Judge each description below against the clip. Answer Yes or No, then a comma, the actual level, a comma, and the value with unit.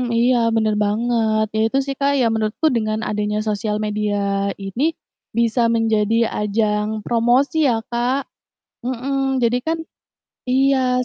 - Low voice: No, high, 230 Hz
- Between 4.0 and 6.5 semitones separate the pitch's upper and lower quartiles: No, average, 3.2 semitones